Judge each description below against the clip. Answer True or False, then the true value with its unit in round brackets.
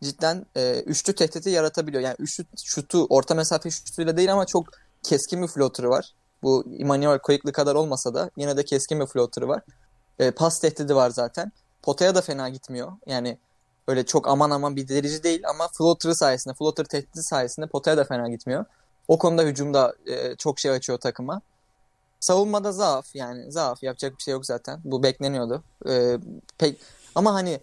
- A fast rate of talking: True (175 wpm)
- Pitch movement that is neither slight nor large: True (4.0 semitones)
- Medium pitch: True (145 Hz)